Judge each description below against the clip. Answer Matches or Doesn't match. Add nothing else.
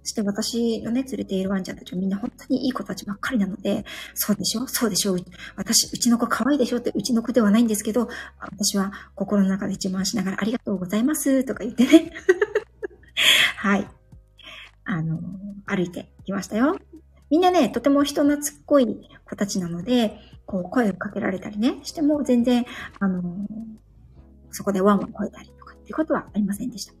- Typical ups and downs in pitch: Matches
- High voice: Matches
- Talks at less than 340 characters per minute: Doesn't match